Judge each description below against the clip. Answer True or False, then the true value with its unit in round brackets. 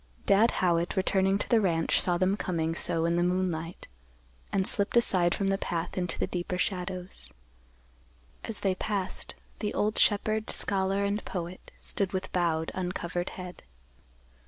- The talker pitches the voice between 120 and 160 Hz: False (185 Hz)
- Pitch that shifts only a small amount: True (2.3 semitones)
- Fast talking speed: False (155 wpm)